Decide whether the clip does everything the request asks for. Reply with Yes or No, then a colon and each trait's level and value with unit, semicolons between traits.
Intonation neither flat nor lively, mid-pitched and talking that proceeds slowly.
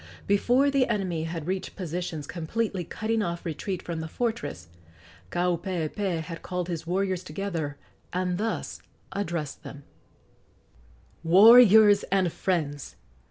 Yes: average, 3.5 semitones; medium, 180 Hz; slow, 115 wpm